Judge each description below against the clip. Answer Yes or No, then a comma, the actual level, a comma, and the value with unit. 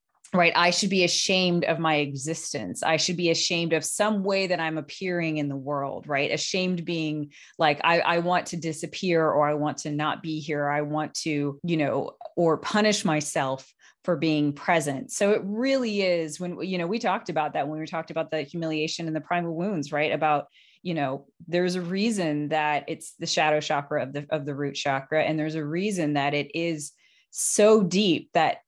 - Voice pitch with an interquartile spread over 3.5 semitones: No, average, 2.9 semitones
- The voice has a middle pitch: Yes, medium, 160 Hz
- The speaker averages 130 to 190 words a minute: No, fast, 205 wpm